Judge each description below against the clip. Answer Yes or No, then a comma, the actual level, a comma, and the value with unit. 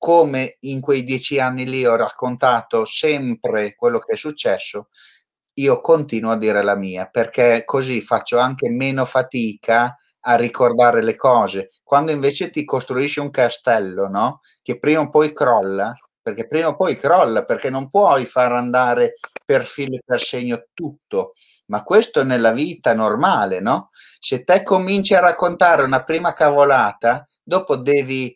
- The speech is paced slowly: No, average, 155 wpm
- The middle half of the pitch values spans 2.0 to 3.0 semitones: No, average, 4.3 semitones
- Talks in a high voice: No, low, 130 Hz